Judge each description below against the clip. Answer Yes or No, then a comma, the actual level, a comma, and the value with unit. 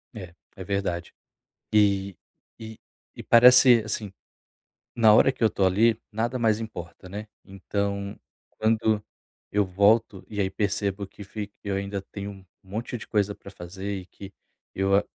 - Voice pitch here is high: No, low, 100 Hz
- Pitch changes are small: Yes, narrow, 2.0 semitones